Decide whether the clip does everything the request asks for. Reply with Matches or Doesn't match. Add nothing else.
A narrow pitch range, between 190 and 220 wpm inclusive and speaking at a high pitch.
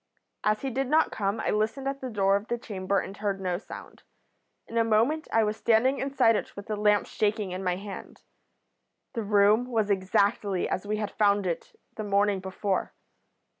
Matches